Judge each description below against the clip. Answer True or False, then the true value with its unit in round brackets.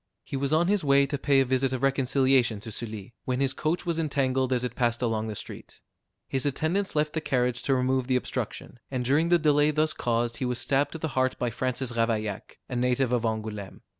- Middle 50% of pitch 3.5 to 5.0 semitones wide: False (2.9 semitones)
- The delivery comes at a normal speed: False (225 wpm)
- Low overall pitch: True (130 Hz)